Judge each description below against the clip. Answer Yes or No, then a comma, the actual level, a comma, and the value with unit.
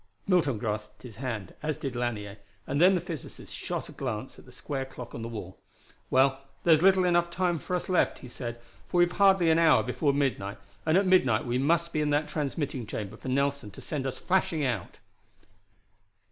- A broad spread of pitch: Yes, wide, 6.0 semitones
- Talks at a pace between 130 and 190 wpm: No, average, 200 wpm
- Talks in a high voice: No, medium, 140 Hz